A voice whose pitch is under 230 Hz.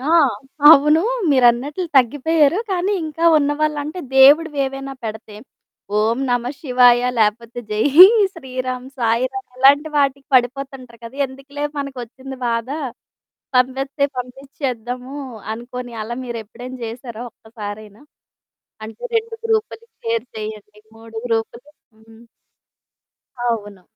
No: very high, 255 Hz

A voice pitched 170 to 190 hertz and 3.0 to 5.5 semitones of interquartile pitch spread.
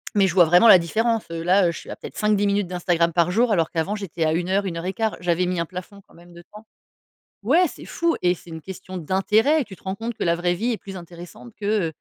Yes: medium, 185 Hz; average, 3.5 semitones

